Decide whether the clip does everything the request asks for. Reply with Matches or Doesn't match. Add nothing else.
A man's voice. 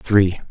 Matches